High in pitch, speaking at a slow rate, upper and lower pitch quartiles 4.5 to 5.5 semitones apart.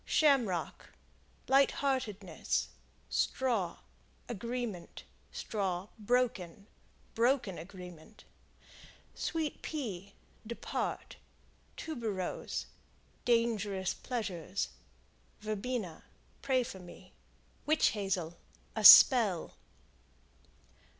Yes: high, 215 Hz; slow, 65 wpm; average, 5.1 semitones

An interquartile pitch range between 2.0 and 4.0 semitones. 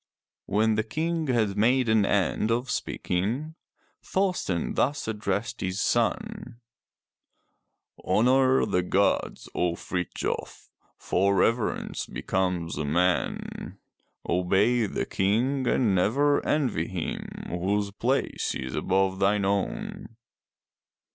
No: average, 4.8 semitones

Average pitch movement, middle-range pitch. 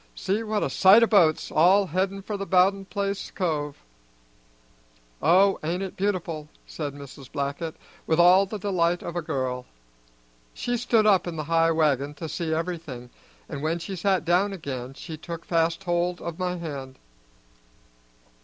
Yes: average, 3.9 semitones; medium, 170 Hz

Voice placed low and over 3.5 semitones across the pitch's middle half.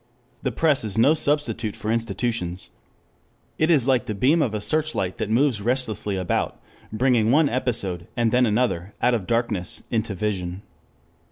Yes: low, 115 Hz; average, 4.1 semitones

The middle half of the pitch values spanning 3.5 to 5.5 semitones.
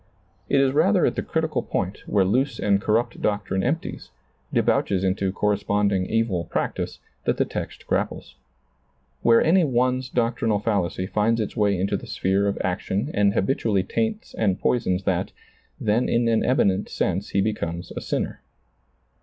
Yes: average, 4.1 semitones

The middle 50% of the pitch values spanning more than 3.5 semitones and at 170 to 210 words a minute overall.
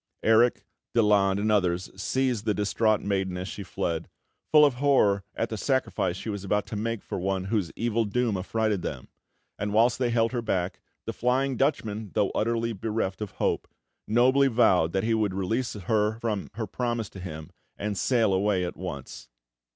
No: average, 3.2 semitones; average, 180 wpm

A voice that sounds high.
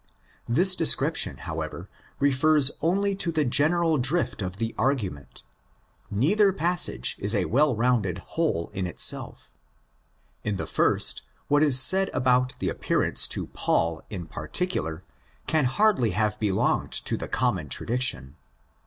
No: low, 130 Hz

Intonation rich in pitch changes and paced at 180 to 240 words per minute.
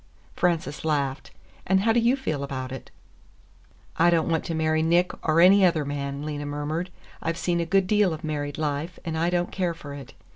No: average, 3.4 semitones; fast, 205 wpm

